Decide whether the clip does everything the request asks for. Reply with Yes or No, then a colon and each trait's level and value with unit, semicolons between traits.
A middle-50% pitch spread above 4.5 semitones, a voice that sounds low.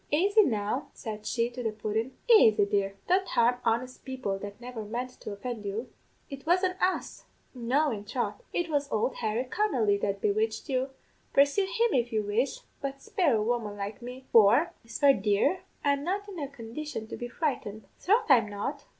No: average, 5.0 semitones; high, 245 Hz